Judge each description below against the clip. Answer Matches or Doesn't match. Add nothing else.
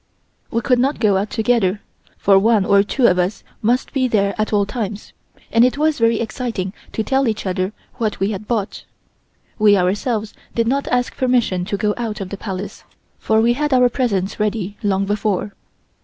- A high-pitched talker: Matches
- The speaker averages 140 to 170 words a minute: Doesn't match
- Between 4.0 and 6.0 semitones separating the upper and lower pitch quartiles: Doesn't match